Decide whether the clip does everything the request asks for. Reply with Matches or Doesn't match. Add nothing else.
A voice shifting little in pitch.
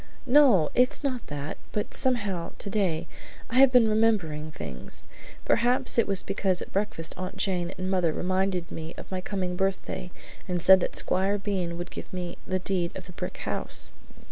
Doesn't match